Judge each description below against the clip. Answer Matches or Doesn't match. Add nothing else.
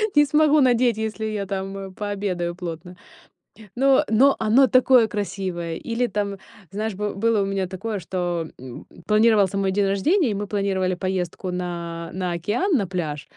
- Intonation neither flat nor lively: Matches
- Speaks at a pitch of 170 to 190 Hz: Doesn't match